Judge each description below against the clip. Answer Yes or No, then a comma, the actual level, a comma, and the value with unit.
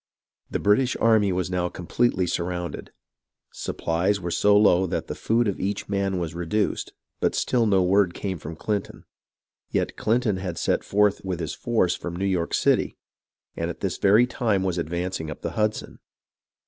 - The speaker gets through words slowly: No, average, 175 wpm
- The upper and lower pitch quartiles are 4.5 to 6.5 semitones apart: No, average, 2.9 semitones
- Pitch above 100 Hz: No, very low, 95 Hz